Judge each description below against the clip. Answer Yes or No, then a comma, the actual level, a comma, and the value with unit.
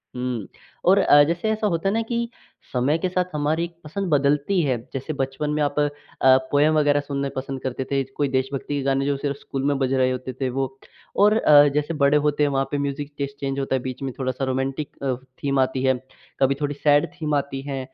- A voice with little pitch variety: Yes, narrow, 2.0 semitones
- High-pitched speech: No, medium, 140 Hz